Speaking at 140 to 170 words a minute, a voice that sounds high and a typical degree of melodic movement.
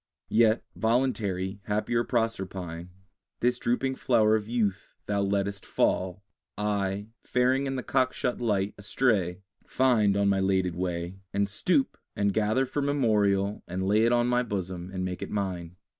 No: average, 150 wpm; low, 105 Hz; average, 3.9 semitones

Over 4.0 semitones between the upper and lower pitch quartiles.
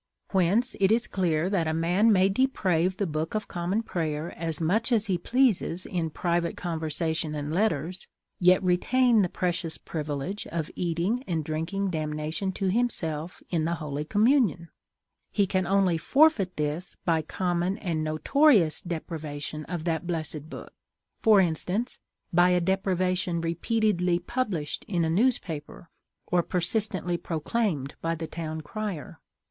No: average, 3.5 semitones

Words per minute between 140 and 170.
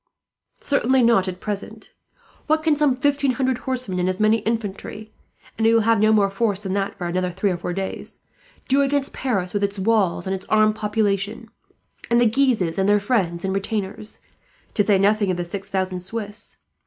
No: average, 195 wpm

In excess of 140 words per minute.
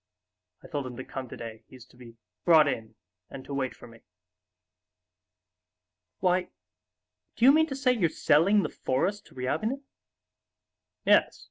Yes: average, 150 wpm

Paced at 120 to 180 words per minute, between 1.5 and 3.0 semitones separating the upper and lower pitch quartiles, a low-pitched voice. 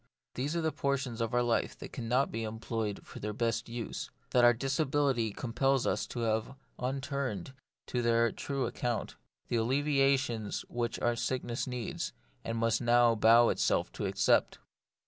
Yes: average, 155 wpm; average, 2.7 semitones; low, 120 Hz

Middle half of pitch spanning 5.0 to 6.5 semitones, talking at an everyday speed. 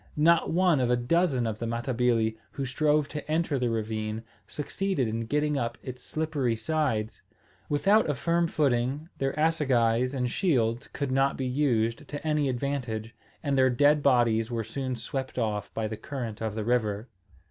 No: average, 4.4 semitones; average, 170 wpm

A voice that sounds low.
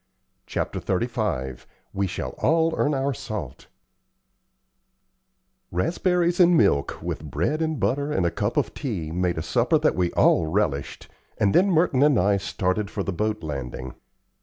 Yes: low, 100 Hz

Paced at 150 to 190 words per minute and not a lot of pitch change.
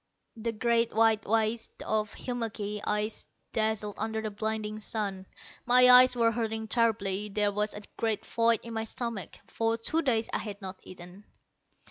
Yes: average, 160 wpm; narrow, 1.6 semitones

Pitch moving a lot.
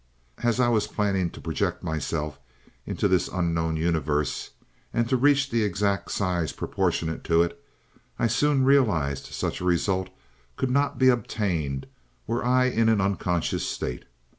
Yes: wide, 6.3 semitones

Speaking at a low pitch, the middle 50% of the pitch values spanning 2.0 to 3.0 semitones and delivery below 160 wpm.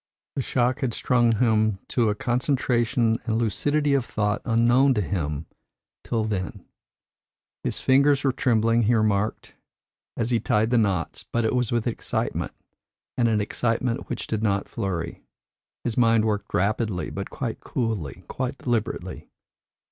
Yes: low, 115 Hz; narrow, 2.6 semitones; average, 150 wpm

